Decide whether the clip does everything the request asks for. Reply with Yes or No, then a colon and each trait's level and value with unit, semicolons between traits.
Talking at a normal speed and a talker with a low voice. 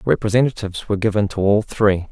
Yes: average, 170 wpm; low, 105 Hz